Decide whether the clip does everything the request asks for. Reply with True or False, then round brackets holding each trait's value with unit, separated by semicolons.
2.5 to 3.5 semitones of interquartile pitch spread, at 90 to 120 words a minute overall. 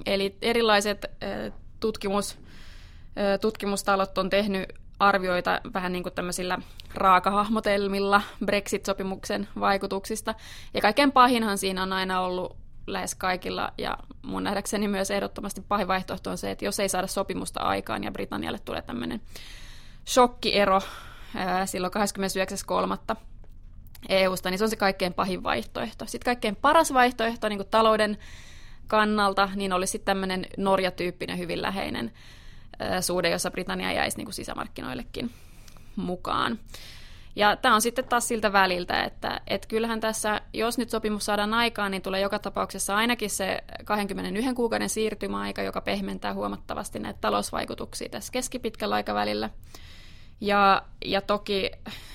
False (2.8 semitones; 130 wpm)